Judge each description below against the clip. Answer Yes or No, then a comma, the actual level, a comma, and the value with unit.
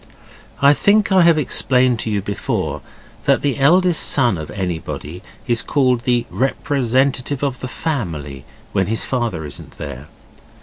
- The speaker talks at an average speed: Yes, average, 145 wpm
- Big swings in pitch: Yes, wide, 6.7 semitones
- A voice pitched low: Yes, low, 125 Hz